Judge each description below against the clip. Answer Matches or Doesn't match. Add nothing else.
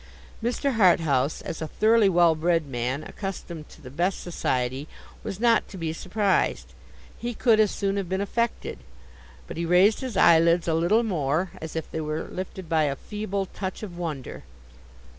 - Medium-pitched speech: Matches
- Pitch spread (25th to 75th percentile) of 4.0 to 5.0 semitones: Matches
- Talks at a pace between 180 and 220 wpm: Doesn't match